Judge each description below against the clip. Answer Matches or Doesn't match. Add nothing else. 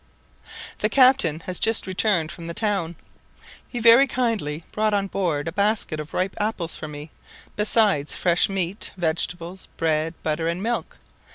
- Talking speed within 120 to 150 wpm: Doesn't match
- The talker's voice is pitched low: Doesn't match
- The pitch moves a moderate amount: Matches